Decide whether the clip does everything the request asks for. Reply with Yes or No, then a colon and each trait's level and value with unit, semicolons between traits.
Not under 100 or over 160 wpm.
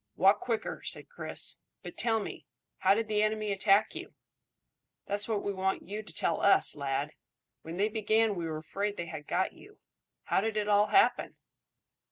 No: average, 185 wpm